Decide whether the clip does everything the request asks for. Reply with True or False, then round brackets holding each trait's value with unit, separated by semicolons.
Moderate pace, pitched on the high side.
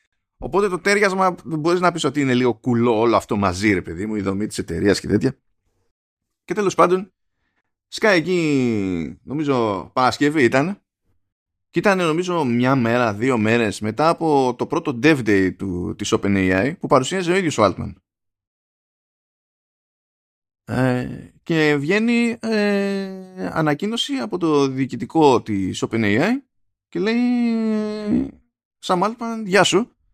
False (135 wpm; 135 Hz)